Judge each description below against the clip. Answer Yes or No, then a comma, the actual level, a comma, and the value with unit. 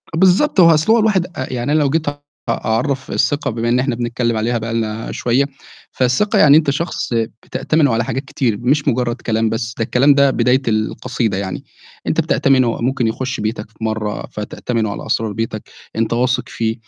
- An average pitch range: Yes, average, 3.7 semitones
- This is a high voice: No, low, 120 Hz